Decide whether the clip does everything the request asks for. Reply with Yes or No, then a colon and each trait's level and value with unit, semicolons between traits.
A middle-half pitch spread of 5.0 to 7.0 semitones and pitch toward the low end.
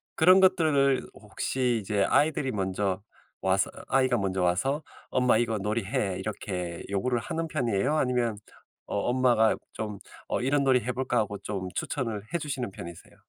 Yes: average, 5.3 semitones; low, 120 Hz